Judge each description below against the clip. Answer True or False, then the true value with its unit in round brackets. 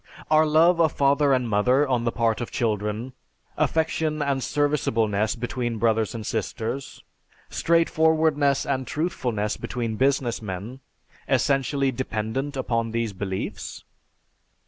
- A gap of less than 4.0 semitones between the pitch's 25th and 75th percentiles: False (4.4 semitones)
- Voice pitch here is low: True (125 Hz)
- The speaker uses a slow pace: True (125 wpm)